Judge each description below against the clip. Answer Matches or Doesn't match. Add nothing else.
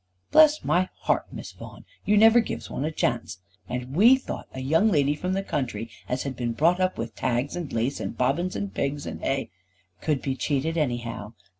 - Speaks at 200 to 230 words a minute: Matches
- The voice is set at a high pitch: Doesn't match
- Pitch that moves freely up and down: Matches